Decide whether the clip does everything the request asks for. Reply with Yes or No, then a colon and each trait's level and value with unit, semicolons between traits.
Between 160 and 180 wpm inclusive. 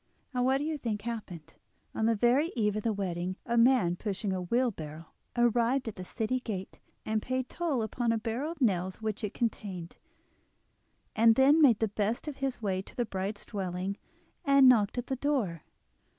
No: average, 190 wpm